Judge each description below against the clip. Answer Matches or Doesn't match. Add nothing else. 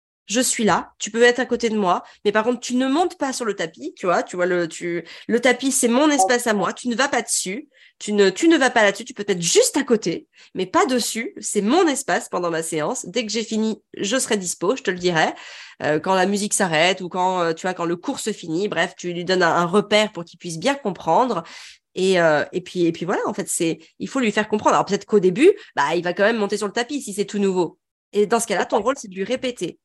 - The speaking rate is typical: Doesn't match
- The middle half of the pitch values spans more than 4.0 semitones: Matches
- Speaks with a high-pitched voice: Matches